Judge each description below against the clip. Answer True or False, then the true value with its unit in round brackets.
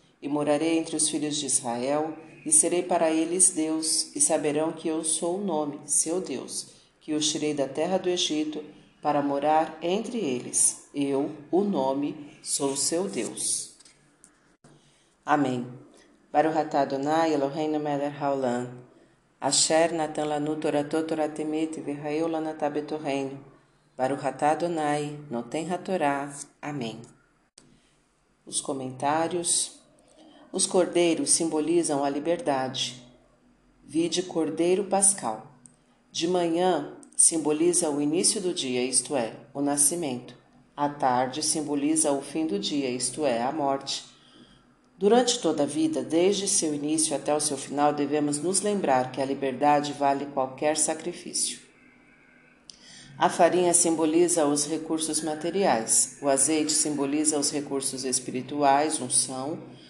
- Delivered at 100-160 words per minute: True (125 wpm)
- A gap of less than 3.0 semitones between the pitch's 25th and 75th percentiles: True (2.6 semitones)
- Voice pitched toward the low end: False (150 Hz)